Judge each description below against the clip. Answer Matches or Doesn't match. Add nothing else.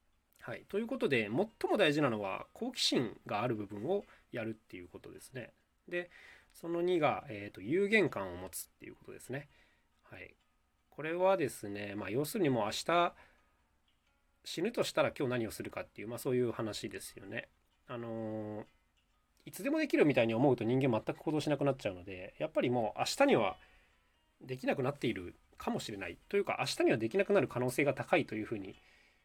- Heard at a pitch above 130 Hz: Doesn't match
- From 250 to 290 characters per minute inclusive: Doesn't match